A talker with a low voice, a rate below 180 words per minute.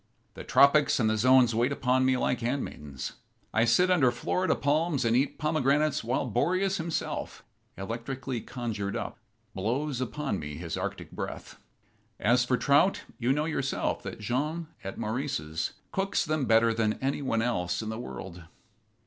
Yes: low, 125 Hz; average, 155 wpm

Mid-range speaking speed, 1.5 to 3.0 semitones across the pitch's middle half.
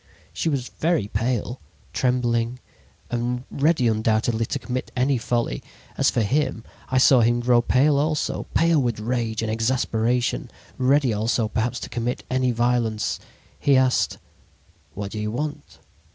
Yes: average, 145 wpm; narrow, 2.4 semitones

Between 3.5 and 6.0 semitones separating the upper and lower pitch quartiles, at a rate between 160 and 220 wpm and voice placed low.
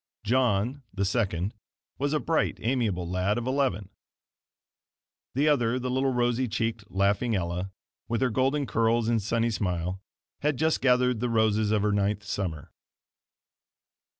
No: average, 4.2 semitones; average, 145 wpm; low, 115 Hz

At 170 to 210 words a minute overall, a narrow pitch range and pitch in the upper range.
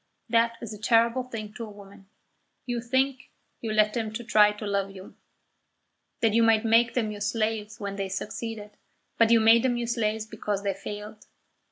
Yes: average, 185 wpm; narrow, 1.9 semitones; high, 220 Hz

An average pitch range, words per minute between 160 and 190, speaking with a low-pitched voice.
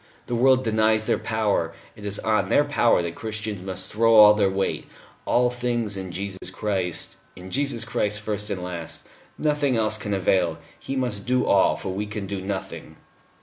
Yes: average, 3.4 semitones; average, 185 wpm; low, 105 Hz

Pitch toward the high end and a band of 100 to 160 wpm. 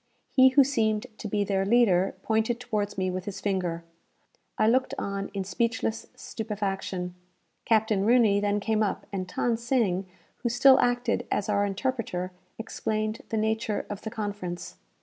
Yes: high, 215 Hz; average, 155 wpm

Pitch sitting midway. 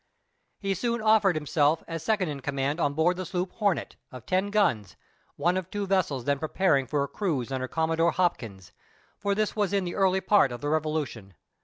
Yes: medium, 165 Hz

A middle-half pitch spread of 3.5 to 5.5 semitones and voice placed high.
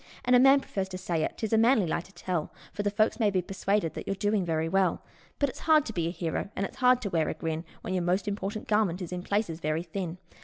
Yes: average, 3.8 semitones; high, 195 Hz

